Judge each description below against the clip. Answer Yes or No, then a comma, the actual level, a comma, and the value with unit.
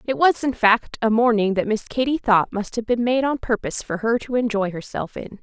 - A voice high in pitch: Yes, high, 225 Hz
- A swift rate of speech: Yes, fast, 245 wpm